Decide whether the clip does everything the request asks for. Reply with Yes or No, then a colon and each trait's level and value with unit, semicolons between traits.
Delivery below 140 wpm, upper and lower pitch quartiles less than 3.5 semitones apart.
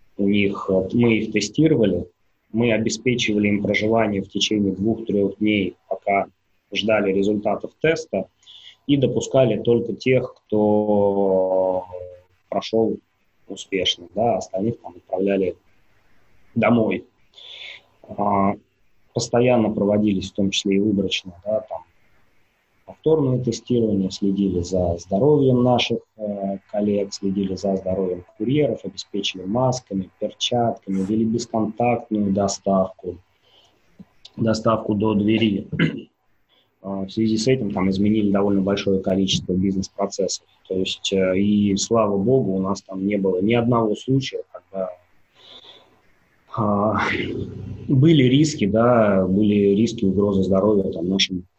Yes: slow, 110 wpm; average, 2.8 semitones